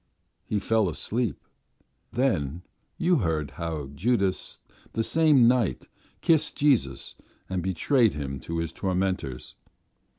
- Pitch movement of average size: No, wide, 7.5 semitones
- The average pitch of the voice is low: Yes, very low, 95 Hz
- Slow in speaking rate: Yes, slow, 110 wpm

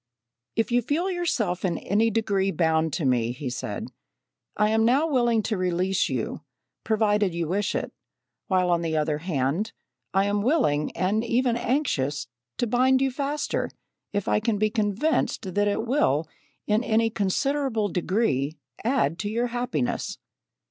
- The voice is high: Yes, high, 210 Hz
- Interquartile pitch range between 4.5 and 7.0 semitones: Yes, average, 5.3 semitones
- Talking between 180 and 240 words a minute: No, average, 155 wpm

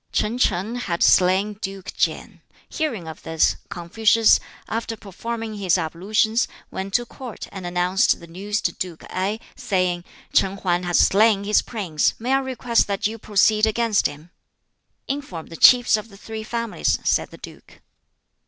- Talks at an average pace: Yes, average, 160 wpm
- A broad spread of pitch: No, average, 3.9 semitones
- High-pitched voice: Yes, high, 205 Hz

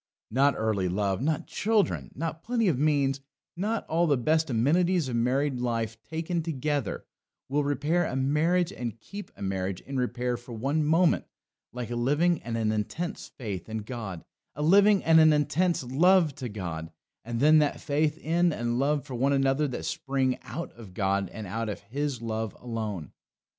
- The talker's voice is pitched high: No, low, 135 Hz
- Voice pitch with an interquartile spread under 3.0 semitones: No, wide, 5.6 semitones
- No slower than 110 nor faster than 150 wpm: No, average, 180 wpm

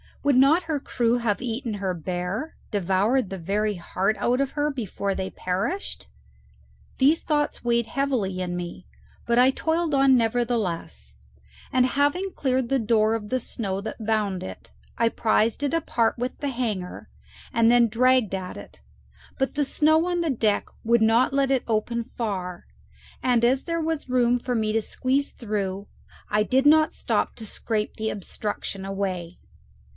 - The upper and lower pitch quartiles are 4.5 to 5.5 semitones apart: Yes, average, 4.9 semitones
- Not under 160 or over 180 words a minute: Yes, average, 165 wpm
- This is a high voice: Yes, high, 230 Hz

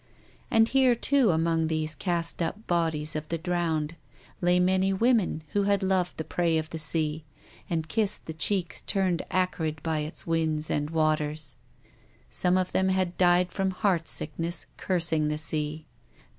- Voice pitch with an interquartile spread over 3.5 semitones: No, average, 3.0 semitones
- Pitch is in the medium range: Yes, medium, 170 Hz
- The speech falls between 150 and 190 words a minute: Yes, average, 160 wpm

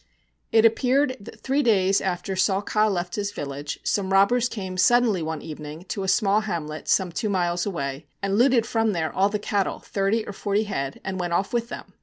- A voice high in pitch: Yes, high, 195 Hz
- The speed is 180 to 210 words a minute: Yes, fast, 205 wpm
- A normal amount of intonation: Yes, average, 3.7 semitones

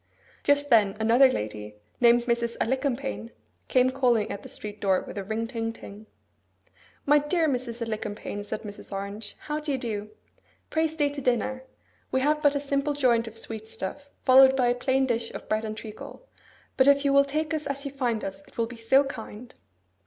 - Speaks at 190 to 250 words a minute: Yes, average, 195 wpm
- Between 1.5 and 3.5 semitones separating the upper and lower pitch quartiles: No, average, 4.2 semitones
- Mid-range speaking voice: No, high, 245 Hz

